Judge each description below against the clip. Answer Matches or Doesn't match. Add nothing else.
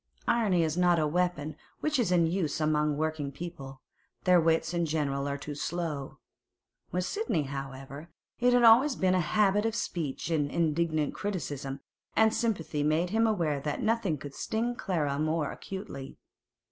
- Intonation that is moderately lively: Matches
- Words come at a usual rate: Matches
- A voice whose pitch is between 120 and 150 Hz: Doesn't match